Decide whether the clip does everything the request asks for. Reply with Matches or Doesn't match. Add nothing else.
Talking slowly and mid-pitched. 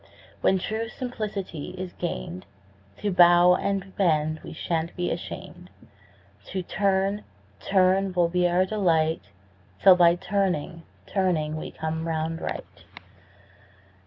Matches